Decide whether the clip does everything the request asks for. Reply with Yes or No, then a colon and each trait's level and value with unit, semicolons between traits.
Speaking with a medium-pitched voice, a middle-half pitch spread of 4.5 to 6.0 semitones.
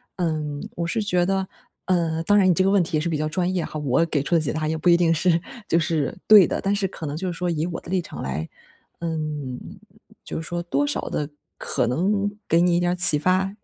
No: medium, 170 Hz; average, 3.0 semitones